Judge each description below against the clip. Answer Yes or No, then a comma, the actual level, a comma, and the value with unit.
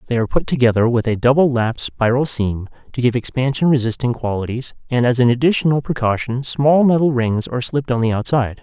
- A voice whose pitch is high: No, low, 125 Hz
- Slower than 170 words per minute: No, average, 195 wpm